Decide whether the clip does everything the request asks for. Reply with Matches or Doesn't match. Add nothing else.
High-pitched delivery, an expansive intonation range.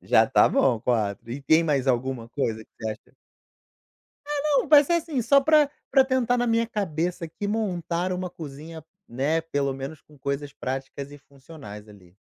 Doesn't match